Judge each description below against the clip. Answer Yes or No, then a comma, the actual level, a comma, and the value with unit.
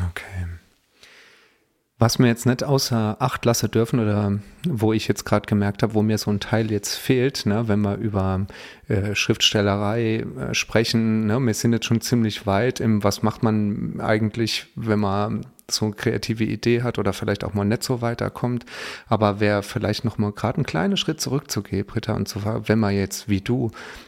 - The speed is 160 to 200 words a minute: Yes, average, 185 wpm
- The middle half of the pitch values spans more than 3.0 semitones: No, narrow, 2.4 semitones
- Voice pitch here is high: No, low, 110 Hz